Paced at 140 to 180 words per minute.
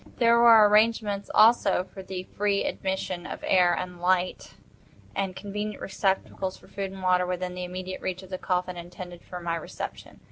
Yes: average, 170 wpm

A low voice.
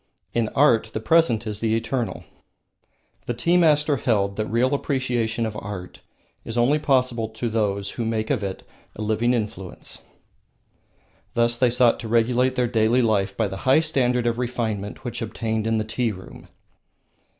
Yes: low, 115 Hz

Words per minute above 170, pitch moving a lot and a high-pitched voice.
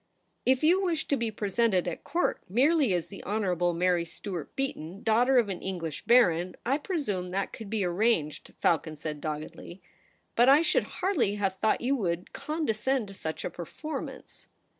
Yes: average, 180 wpm; wide, 6.8 semitones; high, 205 Hz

